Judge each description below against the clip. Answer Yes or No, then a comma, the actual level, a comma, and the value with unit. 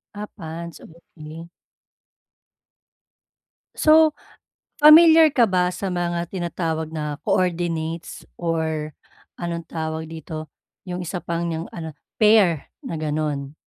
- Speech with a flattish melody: Yes, narrow, 2.1 semitones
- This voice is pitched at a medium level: Yes, medium, 170 Hz